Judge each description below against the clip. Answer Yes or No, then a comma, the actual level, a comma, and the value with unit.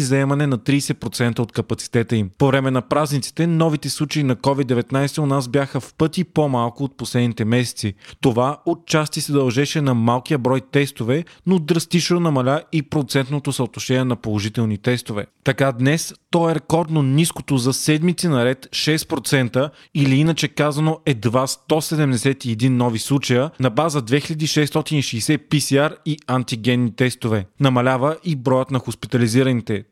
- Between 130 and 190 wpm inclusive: Yes, average, 140 wpm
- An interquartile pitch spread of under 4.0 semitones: Yes, average, 3.6 semitones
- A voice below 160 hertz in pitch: Yes, low, 135 Hz